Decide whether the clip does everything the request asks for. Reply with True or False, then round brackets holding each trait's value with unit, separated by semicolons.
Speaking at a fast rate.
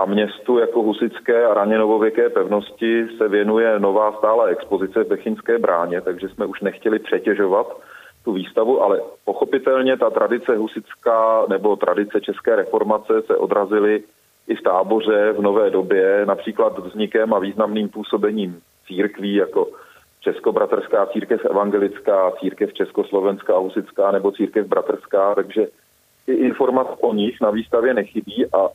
False (135 wpm)